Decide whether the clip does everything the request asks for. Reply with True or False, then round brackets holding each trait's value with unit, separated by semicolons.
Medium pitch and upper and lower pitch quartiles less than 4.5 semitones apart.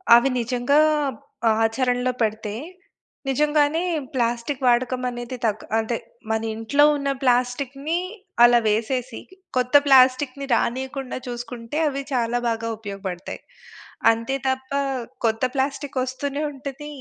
False (250 Hz; 2.9 semitones)